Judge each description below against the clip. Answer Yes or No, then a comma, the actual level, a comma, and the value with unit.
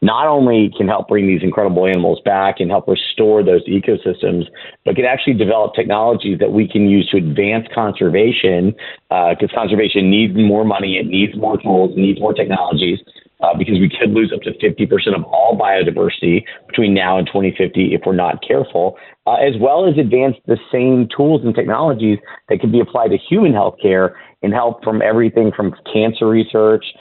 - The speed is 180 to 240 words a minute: Yes, average, 185 wpm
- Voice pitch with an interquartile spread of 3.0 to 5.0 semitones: No, narrow, 2.6 semitones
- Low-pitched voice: Yes, low, 105 Hz